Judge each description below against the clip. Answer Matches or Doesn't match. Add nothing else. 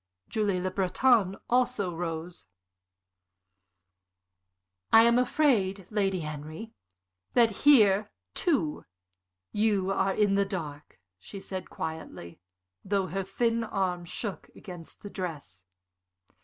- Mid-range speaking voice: Doesn't match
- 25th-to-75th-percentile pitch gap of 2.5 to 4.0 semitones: Matches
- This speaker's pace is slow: Matches